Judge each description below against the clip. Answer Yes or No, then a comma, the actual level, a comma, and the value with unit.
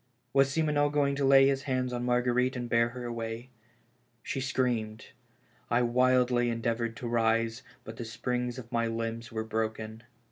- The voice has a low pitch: Yes, low, 120 Hz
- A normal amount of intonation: No, narrow, 2.0 semitones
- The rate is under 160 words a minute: No, average, 170 wpm